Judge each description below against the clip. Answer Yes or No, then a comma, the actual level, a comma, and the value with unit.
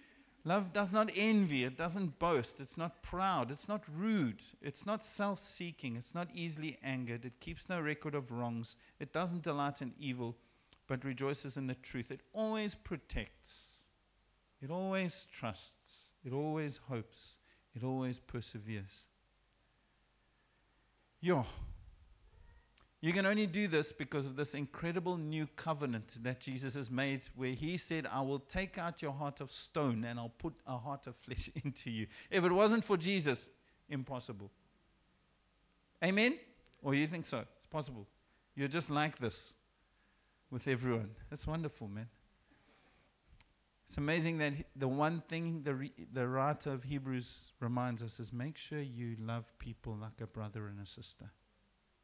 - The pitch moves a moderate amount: No, wide, 5.9 semitones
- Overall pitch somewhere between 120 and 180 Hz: Yes, medium, 140 Hz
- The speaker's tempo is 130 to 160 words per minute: Yes, average, 155 wpm